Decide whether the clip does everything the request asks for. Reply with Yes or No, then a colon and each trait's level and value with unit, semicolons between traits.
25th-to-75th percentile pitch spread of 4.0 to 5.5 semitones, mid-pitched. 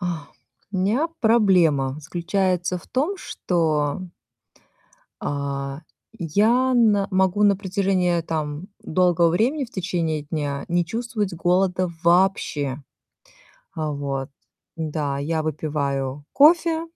Yes: average, 4.9 semitones; medium, 175 Hz